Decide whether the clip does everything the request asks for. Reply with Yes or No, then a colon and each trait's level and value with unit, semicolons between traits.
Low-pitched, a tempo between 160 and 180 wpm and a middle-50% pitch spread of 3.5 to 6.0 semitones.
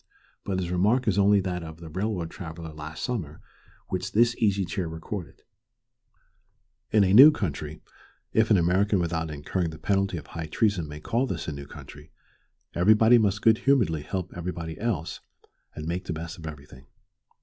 Yes: very low, 90 Hz; average, 170 wpm; average, 4.3 semitones